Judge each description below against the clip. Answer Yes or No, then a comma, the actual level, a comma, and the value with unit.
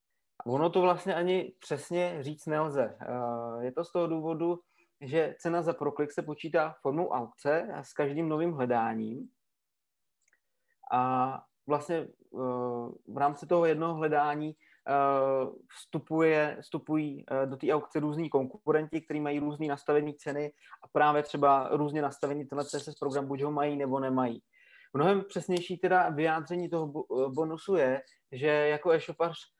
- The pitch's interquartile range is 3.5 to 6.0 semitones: No, average, 2.8 semitones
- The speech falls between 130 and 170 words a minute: Yes, average, 135 wpm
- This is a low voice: No, medium, 150 Hz